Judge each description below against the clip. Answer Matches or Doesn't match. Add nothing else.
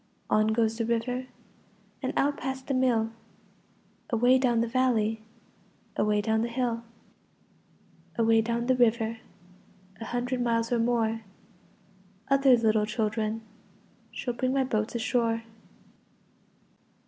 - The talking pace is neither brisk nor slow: Doesn't match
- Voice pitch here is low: Doesn't match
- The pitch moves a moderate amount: Doesn't match